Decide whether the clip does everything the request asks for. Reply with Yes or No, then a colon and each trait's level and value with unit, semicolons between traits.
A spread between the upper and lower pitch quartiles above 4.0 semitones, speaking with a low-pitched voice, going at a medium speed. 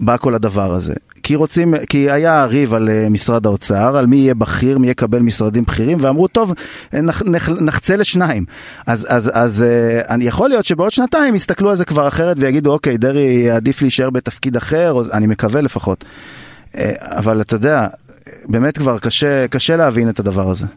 No: average, 5.1 semitones; low, 130 Hz; fast, 180 wpm